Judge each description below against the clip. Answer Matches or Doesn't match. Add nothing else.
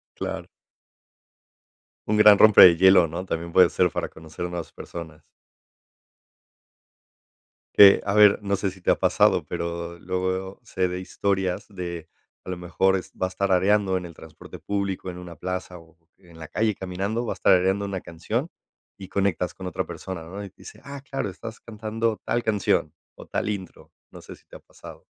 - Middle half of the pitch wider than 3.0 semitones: Doesn't match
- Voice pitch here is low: Matches